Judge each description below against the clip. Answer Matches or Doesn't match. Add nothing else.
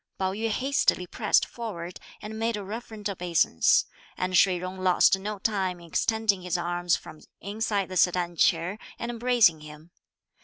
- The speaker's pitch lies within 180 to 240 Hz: Matches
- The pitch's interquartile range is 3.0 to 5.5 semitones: Matches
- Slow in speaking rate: Doesn't match